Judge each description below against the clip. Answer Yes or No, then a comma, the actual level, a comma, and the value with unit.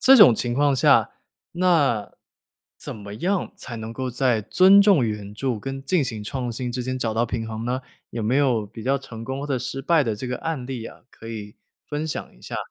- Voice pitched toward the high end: No, low, 125 Hz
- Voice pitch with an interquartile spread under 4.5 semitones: Yes, average, 3.9 semitones